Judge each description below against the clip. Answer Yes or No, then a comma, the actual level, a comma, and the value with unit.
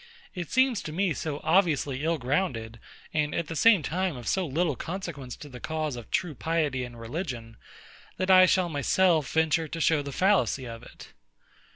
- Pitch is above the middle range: No, medium, 155 Hz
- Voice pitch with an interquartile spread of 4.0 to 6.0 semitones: Yes, average, 5.2 semitones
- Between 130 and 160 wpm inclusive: No, average, 185 wpm